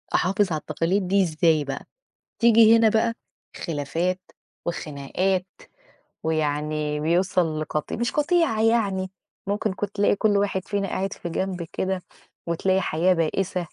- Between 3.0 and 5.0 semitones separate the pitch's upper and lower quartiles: Yes, average, 4.0 semitones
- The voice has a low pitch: No, medium, 185 Hz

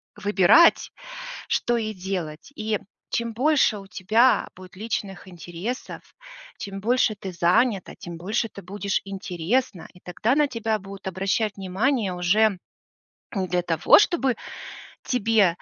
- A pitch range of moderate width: Yes, average, 3.8 semitones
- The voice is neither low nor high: No, high, 200 Hz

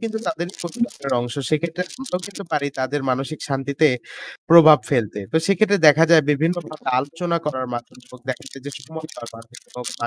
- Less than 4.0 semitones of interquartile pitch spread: No, average, 4.4 semitones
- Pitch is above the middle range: No, medium, 155 Hz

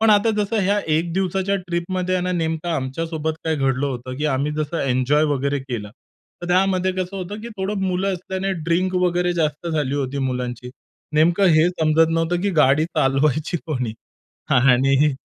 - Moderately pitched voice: Yes, medium, 160 Hz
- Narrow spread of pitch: No, average, 4.9 semitones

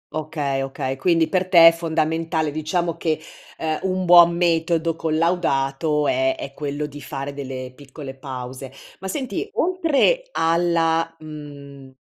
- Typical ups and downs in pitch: Yes, average, 3.4 semitones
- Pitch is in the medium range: Yes, medium, 155 Hz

